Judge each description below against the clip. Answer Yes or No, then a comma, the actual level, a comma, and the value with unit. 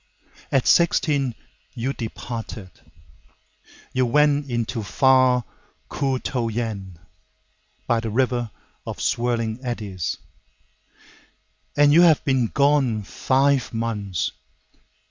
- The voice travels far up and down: No, average, 3.3 semitones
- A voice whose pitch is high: No, low, 120 Hz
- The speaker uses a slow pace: Yes, slow, 85 wpm